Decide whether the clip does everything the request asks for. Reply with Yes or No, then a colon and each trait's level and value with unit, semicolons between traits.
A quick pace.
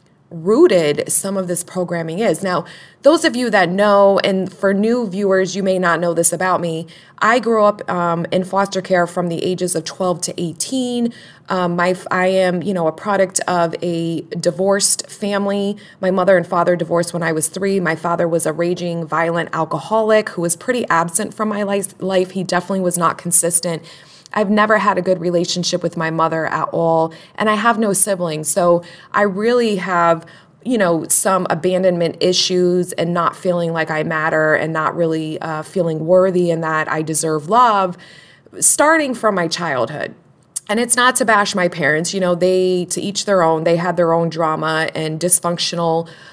No: average, 185 wpm